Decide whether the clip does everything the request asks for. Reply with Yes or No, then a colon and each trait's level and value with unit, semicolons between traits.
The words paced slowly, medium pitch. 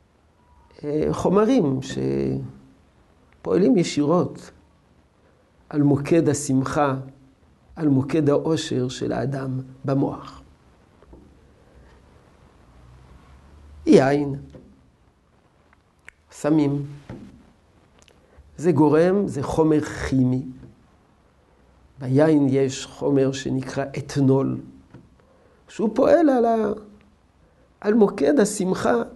No: slow, 65 wpm; low, 130 Hz